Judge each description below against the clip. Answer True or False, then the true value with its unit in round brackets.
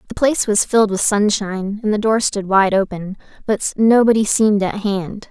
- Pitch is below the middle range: False (205 Hz)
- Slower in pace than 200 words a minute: True (190 wpm)